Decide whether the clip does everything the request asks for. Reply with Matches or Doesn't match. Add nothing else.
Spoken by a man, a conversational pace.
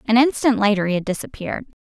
Doesn't match